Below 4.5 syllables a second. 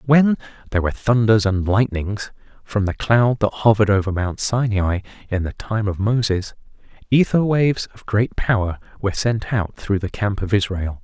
No: 5.0 syllables/s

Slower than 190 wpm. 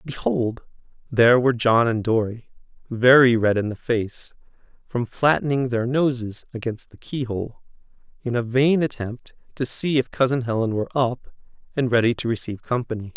Yes: average, 160 wpm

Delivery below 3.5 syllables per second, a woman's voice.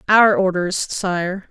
Yes: 3.0 syllables/s; female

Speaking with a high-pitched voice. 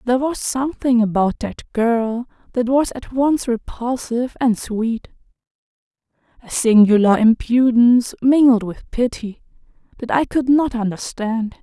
Yes: high, 240 Hz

